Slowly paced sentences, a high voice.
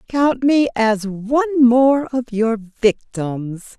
Yes: slow, 125 wpm; high, 240 Hz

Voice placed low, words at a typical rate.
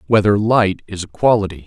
Yes: low, 100 Hz; average, 180 wpm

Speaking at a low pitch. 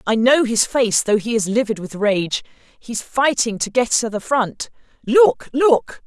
No: high, 230 Hz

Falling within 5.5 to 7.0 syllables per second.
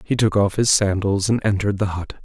Yes: 5.9 syllables/s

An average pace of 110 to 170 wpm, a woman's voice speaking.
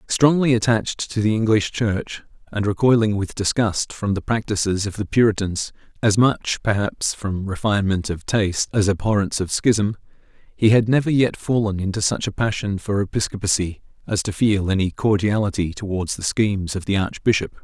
No: average, 160 wpm; male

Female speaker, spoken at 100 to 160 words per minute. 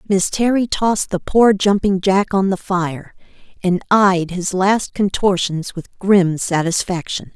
Yes: female; average, 145 wpm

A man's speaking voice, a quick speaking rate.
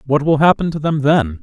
Yes: male; fast, 255 wpm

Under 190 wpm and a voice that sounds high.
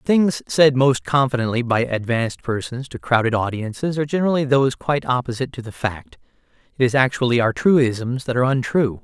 No: average, 180 wpm; low, 130 Hz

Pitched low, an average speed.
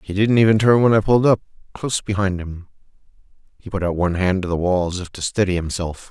No: very low, 95 Hz; fast, 235 wpm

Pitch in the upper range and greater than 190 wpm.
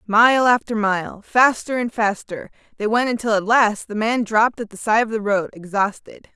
Yes: high, 220 Hz; average, 200 wpm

